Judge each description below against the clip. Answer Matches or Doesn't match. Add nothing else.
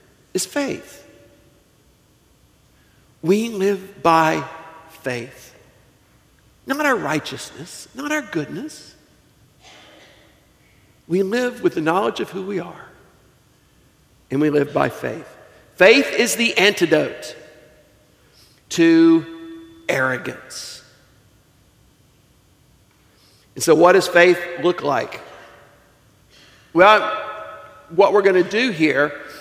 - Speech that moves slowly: Matches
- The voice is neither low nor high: Matches